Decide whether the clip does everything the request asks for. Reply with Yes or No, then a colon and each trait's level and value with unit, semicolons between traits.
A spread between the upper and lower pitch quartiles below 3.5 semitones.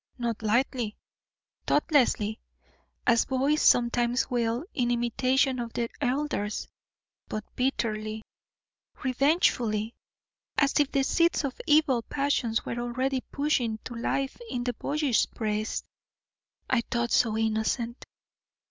Yes: average, 3.0 semitones